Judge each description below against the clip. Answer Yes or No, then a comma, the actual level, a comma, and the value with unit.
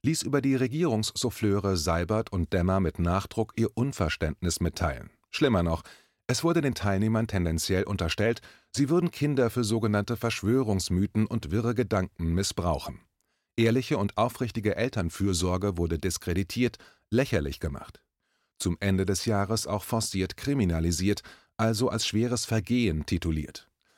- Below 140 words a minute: Yes, slow, 125 wpm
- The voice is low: Yes, low, 105 Hz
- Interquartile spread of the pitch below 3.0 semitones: No, average, 4.4 semitones